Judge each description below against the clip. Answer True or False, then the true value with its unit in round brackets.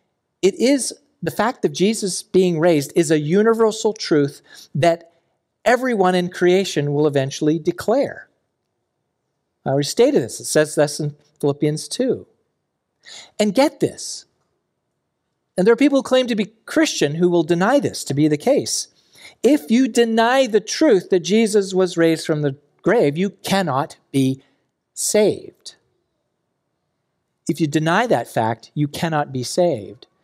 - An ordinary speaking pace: True (145 wpm)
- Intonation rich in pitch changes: True (6.2 semitones)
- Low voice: False (175 Hz)